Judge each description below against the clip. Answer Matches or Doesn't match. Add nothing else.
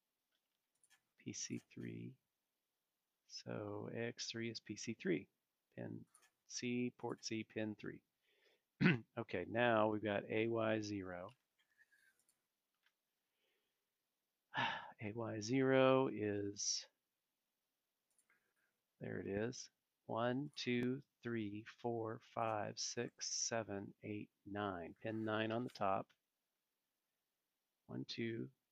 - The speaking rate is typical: Doesn't match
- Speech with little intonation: Doesn't match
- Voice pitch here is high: Doesn't match